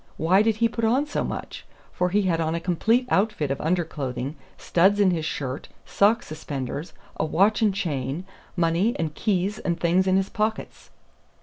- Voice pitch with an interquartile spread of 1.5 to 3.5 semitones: No, average, 4.8 semitones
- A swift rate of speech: No, average, 185 wpm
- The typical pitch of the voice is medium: Yes, medium, 180 Hz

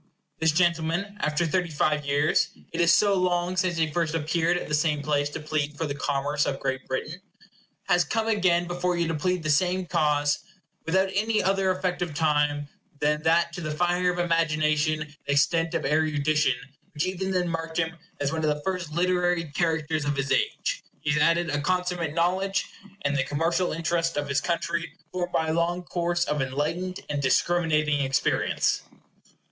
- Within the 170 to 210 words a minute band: Yes, average, 185 wpm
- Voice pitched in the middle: Yes, medium, 165 Hz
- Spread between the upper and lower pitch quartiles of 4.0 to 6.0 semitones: No, average, 2.9 semitones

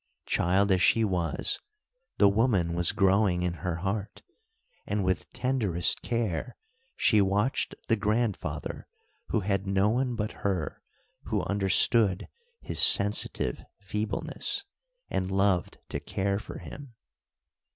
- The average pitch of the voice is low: Yes, low, 100 Hz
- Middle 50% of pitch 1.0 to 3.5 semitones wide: Yes, average, 2.7 semitones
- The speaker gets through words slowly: Yes, slow, 120 wpm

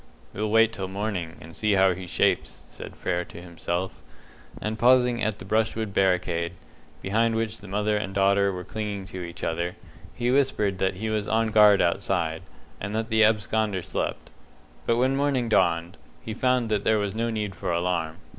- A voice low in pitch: Yes, low, 105 Hz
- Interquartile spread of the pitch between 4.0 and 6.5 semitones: No, average, 3.4 semitones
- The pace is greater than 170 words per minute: Yes, average, 185 wpm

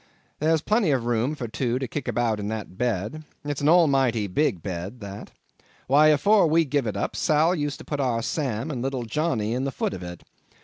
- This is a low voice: Yes, low, 130 Hz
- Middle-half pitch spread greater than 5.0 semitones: Yes, wide, 5.4 semitones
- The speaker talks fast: Yes, fast, 215 wpm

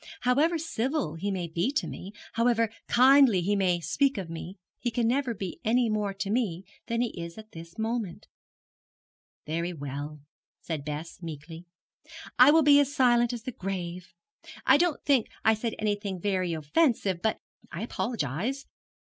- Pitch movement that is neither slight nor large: No, wide, 6.3 semitones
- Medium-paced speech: Yes, average, 165 wpm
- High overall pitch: Yes, high, 210 Hz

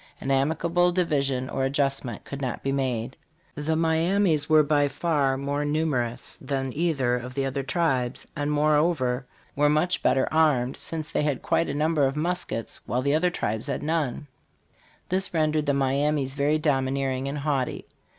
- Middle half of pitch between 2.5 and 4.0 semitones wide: Yes, average, 2.8 semitones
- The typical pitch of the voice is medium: Yes, medium, 145 Hz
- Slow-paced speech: No, average, 165 wpm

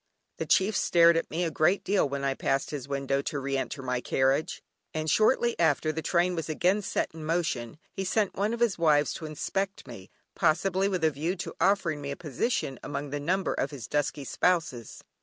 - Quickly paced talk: Yes, fast, 210 wpm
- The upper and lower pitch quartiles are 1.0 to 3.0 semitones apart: No, average, 4.6 semitones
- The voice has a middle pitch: Yes, medium, 155 Hz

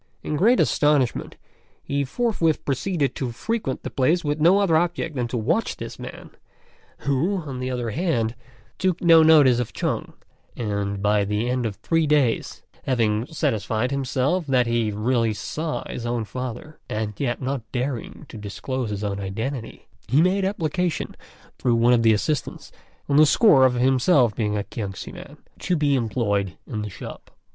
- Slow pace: No, average, 170 wpm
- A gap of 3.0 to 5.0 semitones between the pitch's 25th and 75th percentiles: No, wide, 5.4 semitones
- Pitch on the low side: Yes, low, 130 Hz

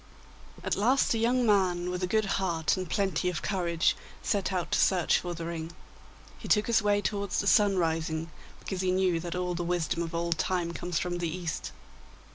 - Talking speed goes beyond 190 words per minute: Yes, average, 200 wpm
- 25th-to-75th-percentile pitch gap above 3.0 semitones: No, average, 2.7 semitones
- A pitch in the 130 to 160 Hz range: No, medium, 180 Hz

